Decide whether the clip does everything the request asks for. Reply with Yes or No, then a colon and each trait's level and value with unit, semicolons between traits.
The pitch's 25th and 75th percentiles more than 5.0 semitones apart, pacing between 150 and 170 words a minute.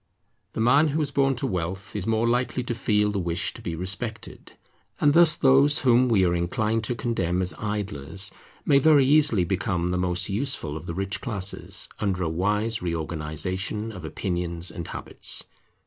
No: wide, 5.6 semitones; average, 180 wpm